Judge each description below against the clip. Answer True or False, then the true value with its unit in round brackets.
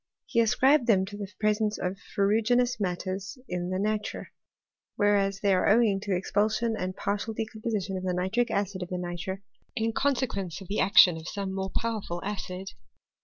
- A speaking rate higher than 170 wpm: True (180 wpm)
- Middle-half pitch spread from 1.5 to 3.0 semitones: True (2.6 semitones)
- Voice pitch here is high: True (200 Hz)